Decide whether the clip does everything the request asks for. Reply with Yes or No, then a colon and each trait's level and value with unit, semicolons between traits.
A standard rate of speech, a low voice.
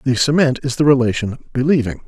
Yes: average, 175 wpm; low, 130 Hz